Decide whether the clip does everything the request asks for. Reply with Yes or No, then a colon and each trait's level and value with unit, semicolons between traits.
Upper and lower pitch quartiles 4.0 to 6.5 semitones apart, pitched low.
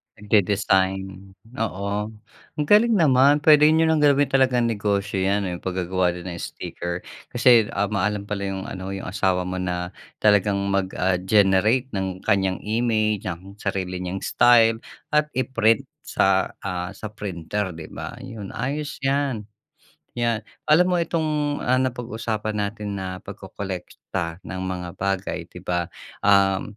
Yes: average, 4.4 semitones; low, 100 Hz